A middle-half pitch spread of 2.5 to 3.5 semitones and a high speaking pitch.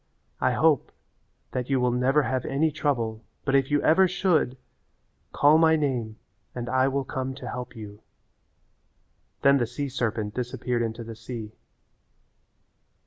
No: average, 3.0 semitones; low, 130 Hz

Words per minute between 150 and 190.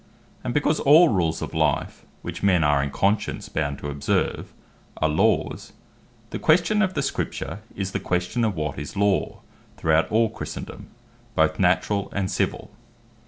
Yes: average, 160 wpm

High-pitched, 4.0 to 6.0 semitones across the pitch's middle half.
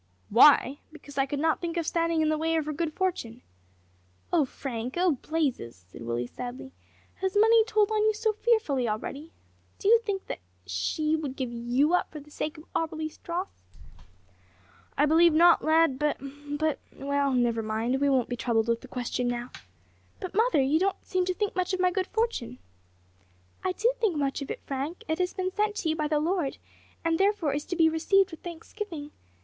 Yes: very high, 315 Hz; average, 5.3 semitones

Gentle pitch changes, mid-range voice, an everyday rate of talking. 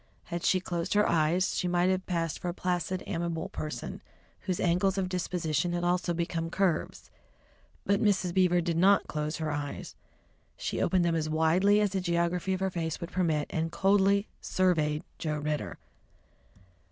Yes: narrow, 2.3 semitones; medium, 175 Hz; average, 170 wpm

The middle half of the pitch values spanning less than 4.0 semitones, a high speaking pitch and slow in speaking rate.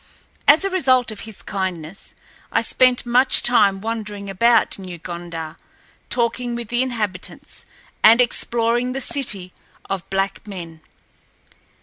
No: average, 4.4 semitones; high, 220 Hz; slow, 125 wpm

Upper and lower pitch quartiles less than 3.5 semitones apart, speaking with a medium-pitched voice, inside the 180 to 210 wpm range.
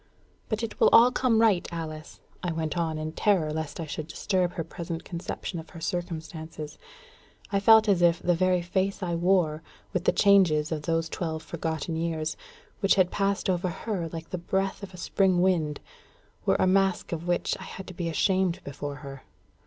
Yes: average, 3.0 semitones; medium, 175 Hz; average, 190 wpm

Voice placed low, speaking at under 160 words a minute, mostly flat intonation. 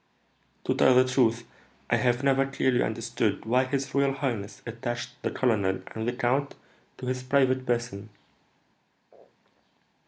Yes: low, 125 Hz; slow, 135 wpm; narrow, 2.1 semitones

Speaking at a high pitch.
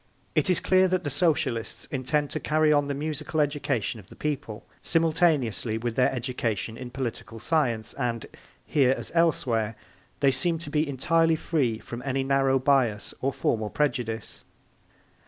No: low, 135 Hz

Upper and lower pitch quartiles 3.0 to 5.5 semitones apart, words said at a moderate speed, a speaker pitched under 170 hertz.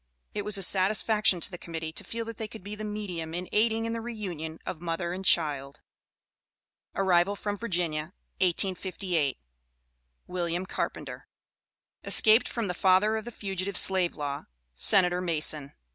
No: average, 3.8 semitones; average, 155 wpm; medium, 185 Hz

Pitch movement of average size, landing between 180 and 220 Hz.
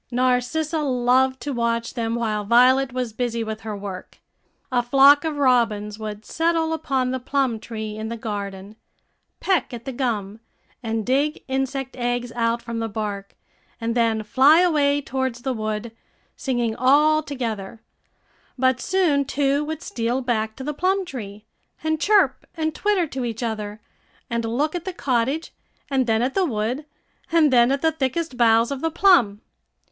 No: average, 4.1 semitones; very high, 250 Hz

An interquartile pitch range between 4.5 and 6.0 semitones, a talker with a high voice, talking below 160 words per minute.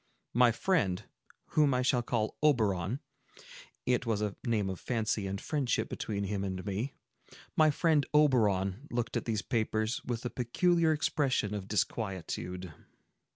No: average, 4.9 semitones; low, 115 Hz; slow, 135 wpm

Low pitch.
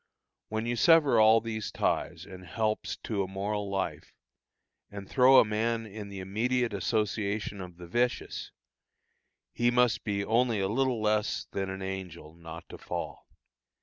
Yes: low, 105 Hz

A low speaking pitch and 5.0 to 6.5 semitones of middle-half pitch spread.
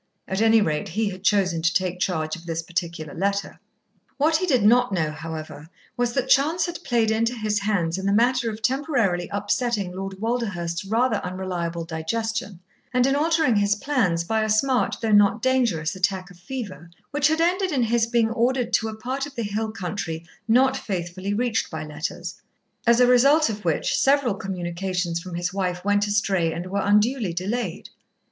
No: high, 205 Hz; wide, 5.4 semitones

